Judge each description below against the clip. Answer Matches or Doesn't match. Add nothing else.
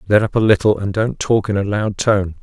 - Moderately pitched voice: Doesn't match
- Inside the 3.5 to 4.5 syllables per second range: Doesn't match